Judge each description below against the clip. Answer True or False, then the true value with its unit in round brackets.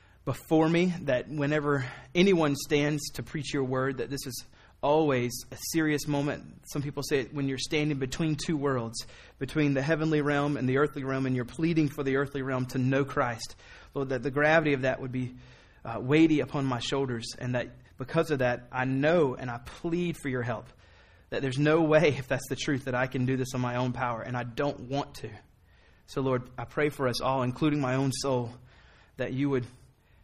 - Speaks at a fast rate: True (210 wpm)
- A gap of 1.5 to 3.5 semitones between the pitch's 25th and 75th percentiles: True (2.8 semitones)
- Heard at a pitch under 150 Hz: True (135 Hz)